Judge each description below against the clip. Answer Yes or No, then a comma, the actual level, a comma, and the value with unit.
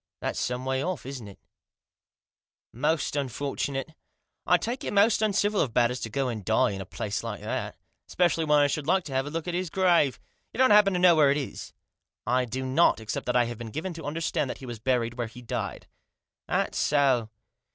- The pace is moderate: No, fast, 230 wpm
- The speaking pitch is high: No, medium, 140 Hz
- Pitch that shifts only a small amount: No, wide, 5.5 semitones